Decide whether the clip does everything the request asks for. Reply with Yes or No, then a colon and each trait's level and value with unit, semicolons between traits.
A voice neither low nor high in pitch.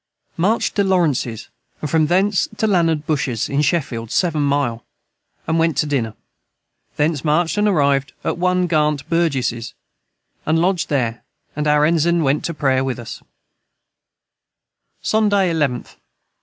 Yes: medium, 150 Hz